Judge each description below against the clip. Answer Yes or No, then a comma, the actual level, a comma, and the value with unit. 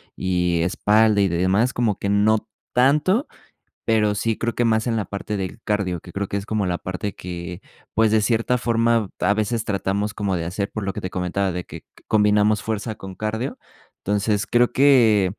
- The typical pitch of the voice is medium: No, low, 105 Hz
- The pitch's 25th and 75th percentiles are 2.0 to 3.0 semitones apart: Yes, average, 2.7 semitones